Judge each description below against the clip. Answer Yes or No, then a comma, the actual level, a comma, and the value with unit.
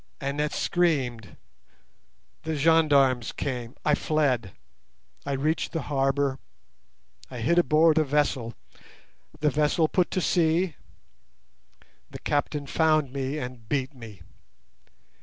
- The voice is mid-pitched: Yes, medium, 145 Hz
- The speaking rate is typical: No, slow, 110 wpm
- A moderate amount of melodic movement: Yes, average, 3.2 semitones